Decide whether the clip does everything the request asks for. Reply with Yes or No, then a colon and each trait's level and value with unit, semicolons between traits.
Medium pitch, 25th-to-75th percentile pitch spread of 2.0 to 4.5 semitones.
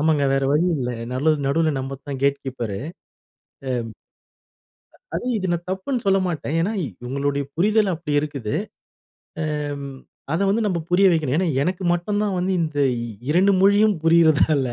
No: medium, 160 Hz; average, 5.1 semitones